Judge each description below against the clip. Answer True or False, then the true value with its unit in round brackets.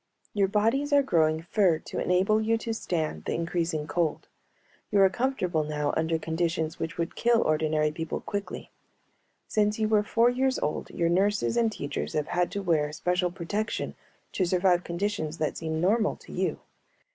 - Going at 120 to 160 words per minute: False (170 wpm)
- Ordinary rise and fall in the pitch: True (4.8 semitones)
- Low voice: False (180 Hz)